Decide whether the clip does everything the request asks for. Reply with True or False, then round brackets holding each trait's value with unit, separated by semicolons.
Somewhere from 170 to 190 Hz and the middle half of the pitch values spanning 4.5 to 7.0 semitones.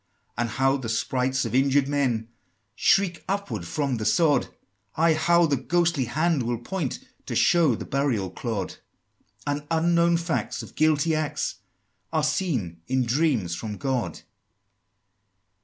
False (140 Hz; 5.2 semitones)